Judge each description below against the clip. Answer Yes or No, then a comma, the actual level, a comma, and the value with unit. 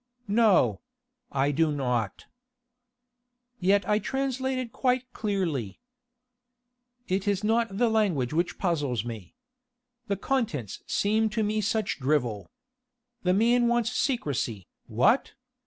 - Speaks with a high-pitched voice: Yes, high, 200 Hz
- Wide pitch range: Yes, wide, 8.4 semitones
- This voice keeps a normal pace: No, slow, 110 wpm